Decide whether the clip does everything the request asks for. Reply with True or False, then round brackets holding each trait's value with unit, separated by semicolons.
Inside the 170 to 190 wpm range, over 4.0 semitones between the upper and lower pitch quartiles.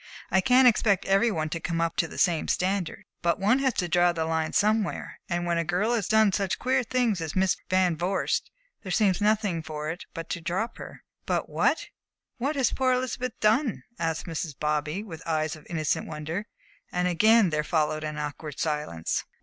False (200 wpm; 5.0 semitones)